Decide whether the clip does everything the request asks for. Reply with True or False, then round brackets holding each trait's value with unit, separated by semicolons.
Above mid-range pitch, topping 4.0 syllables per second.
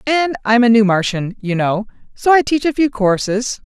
True (230 Hz; 4.9 syllables/s)